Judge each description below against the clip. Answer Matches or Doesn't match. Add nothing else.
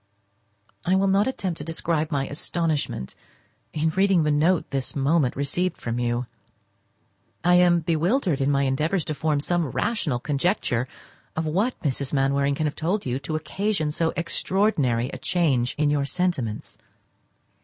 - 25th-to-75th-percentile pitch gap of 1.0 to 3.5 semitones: Doesn't match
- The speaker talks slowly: Doesn't match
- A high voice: Doesn't match